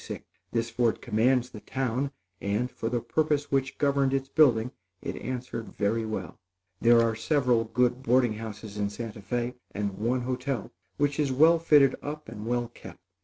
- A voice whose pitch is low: Yes, low, 125 Hz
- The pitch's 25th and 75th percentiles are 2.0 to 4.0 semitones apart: Yes, average, 3.2 semitones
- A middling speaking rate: Yes, average, 170 wpm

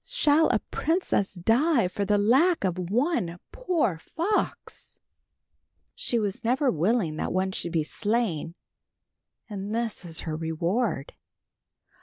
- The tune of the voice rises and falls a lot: Yes, wide, 6.6 semitones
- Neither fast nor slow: No, slow, 125 wpm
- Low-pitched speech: No, high, 210 Hz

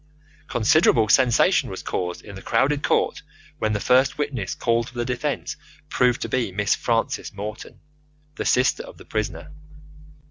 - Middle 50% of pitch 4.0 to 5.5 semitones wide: No, average, 3.4 semitones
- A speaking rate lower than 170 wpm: Yes, average, 155 wpm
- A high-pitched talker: No, low, 115 Hz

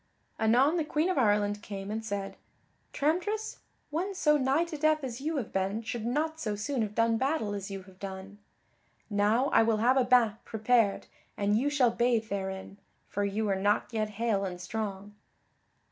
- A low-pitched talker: No, high, 225 Hz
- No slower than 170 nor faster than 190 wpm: Yes, average, 185 wpm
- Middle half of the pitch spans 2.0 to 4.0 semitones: No, average, 5.0 semitones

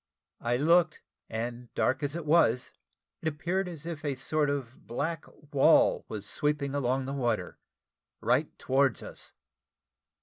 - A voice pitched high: No, medium, 140 Hz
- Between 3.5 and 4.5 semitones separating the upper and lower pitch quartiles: Yes, average, 4.0 semitones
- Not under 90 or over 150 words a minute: Yes, average, 140 wpm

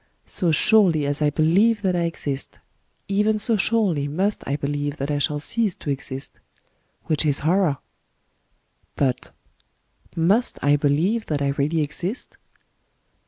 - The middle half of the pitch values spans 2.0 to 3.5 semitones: No, wide, 5.5 semitones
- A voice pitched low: No, medium, 155 Hz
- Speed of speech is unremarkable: Yes, average, 150 wpm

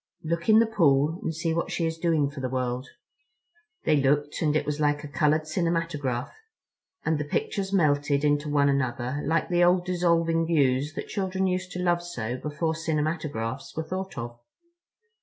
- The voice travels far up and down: No, average, 3.1 semitones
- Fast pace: No, average, 175 wpm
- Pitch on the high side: No, medium, 155 Hz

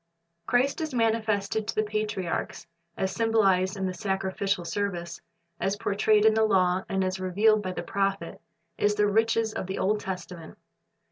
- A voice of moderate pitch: No, high, 200 Hz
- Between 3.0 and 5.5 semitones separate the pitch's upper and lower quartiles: No, narrow, 2.5 semitones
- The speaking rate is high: No, average, 160 wpm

